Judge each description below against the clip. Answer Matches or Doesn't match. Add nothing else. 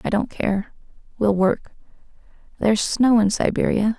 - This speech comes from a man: Doesn't match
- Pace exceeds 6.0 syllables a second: Doesn't match